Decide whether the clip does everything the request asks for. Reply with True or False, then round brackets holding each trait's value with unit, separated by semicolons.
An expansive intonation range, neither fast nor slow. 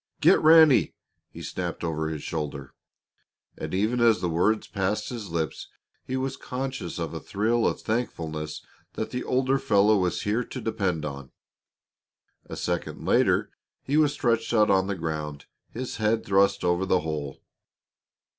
True (6.5 semitones; 155 wpm)